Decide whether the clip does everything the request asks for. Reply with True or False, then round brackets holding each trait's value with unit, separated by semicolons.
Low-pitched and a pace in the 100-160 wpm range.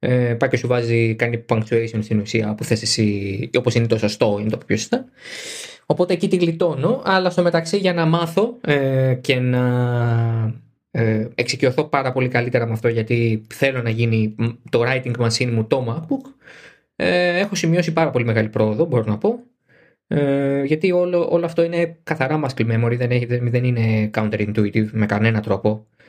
False (125 Hz; 170 wpm)